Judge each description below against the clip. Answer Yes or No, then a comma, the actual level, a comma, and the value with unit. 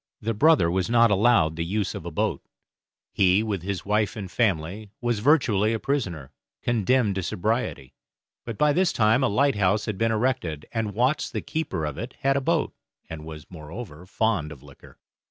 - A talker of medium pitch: No, low, 105 Hz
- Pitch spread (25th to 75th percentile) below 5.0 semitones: No, wide, 5.4 semitones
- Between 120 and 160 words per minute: No, average, 185 wpm